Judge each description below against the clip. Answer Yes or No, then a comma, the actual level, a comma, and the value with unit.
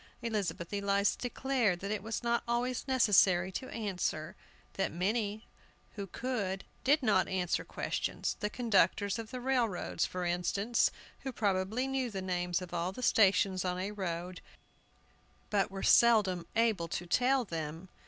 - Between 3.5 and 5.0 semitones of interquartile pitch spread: Yes, average, 4.4 semitones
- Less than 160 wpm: Yes, average, 150 wpm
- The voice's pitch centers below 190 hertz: No, high, 200 Hz